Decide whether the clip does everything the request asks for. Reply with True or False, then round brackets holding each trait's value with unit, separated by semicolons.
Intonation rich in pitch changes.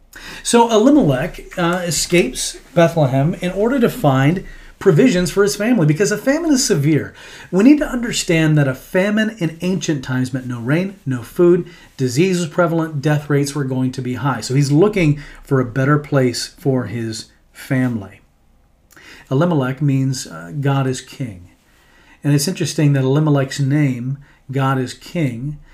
False (5.0 semitones)